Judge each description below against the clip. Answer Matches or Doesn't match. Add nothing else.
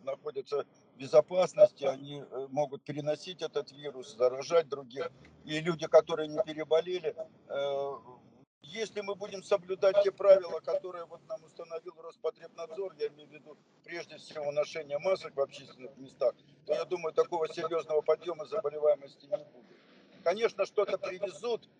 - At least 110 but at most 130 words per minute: Doesn't match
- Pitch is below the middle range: Doesn't match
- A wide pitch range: Doesn't match